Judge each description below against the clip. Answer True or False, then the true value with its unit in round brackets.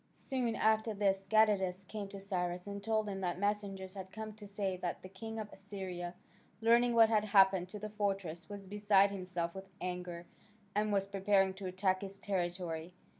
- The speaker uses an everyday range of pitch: False (2.0 semitones)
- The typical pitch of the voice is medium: False (195 Hz)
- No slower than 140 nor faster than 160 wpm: False (180 wpm)